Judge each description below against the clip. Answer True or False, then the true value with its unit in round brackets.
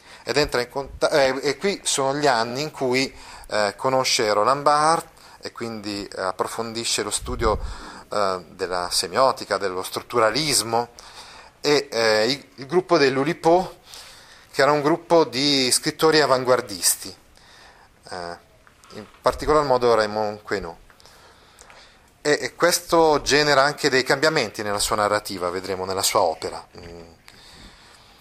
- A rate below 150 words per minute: True (125 wpm)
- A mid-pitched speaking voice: False (130 Hz)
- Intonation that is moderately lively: False (5.9 semitones)